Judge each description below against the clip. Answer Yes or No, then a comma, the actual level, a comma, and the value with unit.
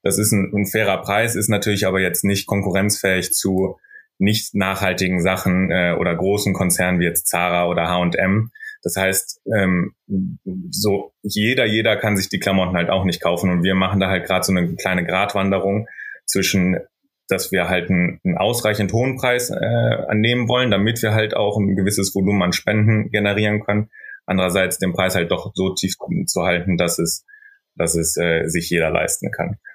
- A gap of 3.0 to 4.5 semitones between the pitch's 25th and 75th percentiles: No, narrow, 2.5 semitones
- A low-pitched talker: Yes, very low, 95 Hz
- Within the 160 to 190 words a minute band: Yes, average, 180 wpm